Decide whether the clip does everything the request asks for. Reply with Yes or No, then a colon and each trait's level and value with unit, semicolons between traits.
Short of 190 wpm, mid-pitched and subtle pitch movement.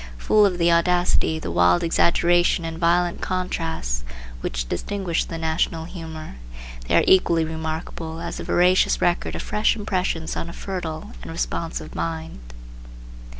Yes: average, 145 wpm; medium, 165 Hz; narrow, 1.8 semitones